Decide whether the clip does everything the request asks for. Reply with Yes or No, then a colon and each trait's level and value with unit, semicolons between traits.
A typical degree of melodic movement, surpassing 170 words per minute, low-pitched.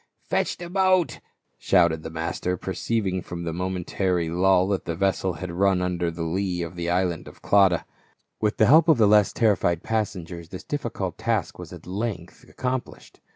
Yes: average, 3.5 semitones; average, 185 wpm; very low, 95 Hz